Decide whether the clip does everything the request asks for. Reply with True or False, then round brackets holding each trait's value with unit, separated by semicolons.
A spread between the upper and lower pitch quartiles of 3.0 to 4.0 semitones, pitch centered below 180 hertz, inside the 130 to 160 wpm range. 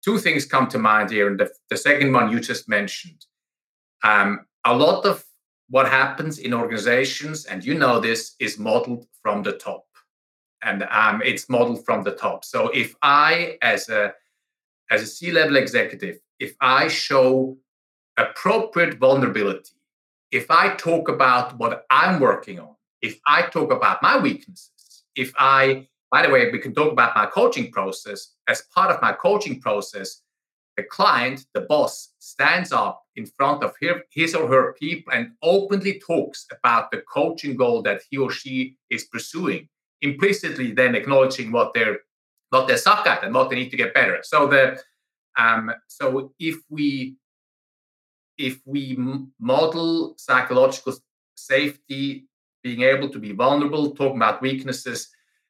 False (4.8 semitones; 140 Hz; 155 wpm)